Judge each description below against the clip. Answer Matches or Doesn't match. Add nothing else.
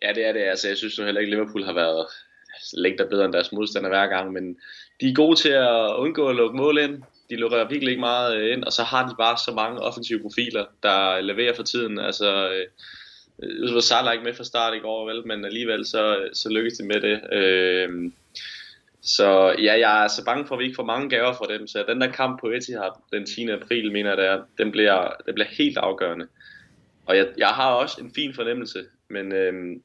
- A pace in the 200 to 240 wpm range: Matches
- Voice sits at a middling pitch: Doesn't match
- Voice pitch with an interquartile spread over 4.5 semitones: Doesn't match